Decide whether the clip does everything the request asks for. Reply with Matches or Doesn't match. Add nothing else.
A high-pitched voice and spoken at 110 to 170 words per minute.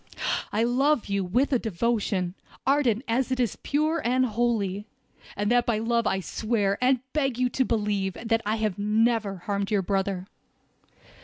Matches